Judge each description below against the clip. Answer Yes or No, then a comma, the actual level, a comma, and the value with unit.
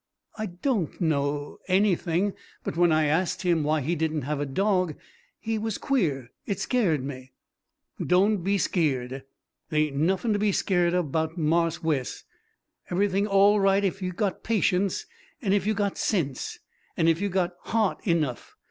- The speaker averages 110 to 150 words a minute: No, average, 165 wpm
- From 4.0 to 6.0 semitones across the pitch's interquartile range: Yes, average, 4.4 semitones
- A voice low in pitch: No, medium, 175 Hz